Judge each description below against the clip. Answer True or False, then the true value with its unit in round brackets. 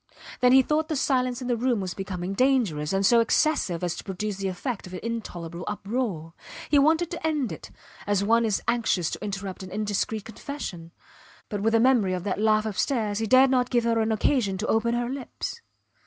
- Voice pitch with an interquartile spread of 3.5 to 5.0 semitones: True (4.6 semitones)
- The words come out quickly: True (210 wpm)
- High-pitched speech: True (220 Hz)